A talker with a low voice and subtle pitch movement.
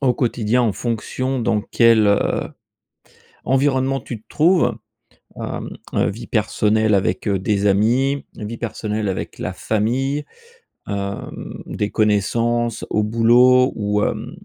No: low, 115 Hz; average, 3.3 semitones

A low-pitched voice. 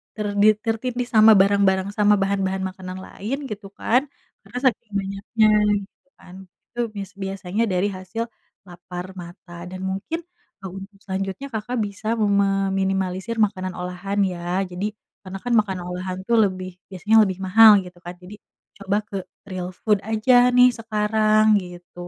No: high, 195 Hz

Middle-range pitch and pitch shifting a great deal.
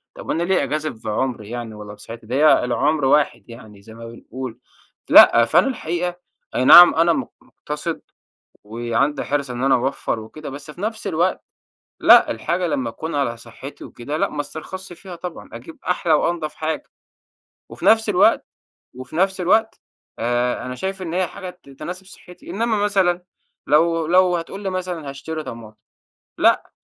Yes: medium, 155 Hz; wide, 6.4 semitones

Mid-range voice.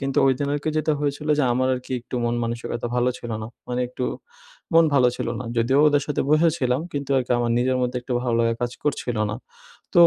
No: low, 130 Hz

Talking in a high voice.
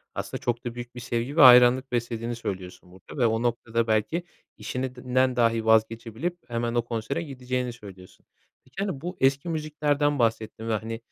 No: low, 120 Hz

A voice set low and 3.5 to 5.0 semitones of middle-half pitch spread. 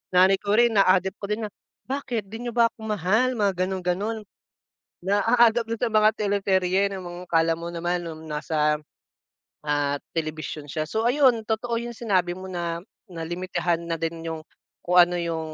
No: medium, 185 Hz; average, 4.6 semitones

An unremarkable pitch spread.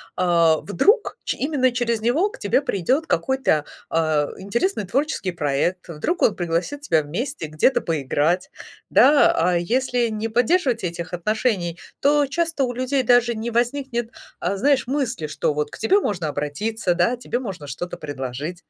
No: wide, 7.7 semitones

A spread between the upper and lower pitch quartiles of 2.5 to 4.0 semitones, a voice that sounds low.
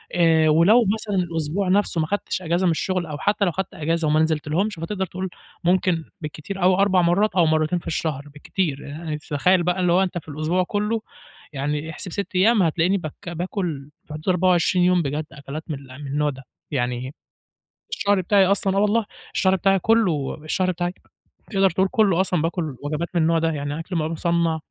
No: average, 3.5 semitones; medium, 170 Hz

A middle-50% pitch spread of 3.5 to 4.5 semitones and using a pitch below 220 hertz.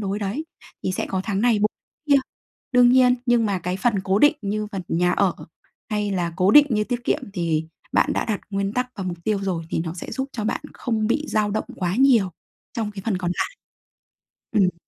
Yes: average, 4.1 semitones; high, 205 Hz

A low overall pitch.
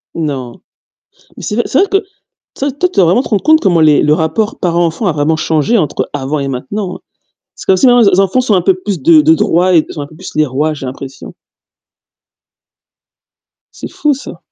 No: medium, 170 Hz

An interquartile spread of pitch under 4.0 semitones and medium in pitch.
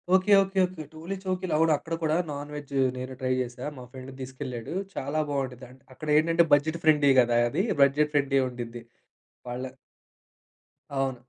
Yes: average, 3.6 semitones; medium, 145 Hz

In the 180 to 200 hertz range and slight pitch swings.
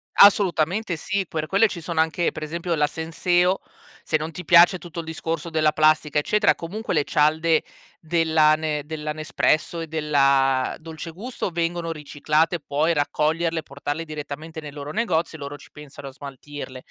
No: medium, 160 Hz; narrow, 2.1 semitones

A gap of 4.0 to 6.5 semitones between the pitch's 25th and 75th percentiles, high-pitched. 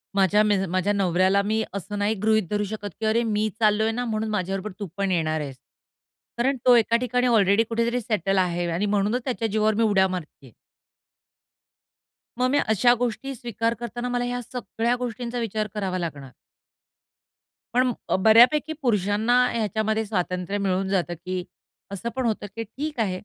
No: average, 3.5 semitones; high, 215 Hz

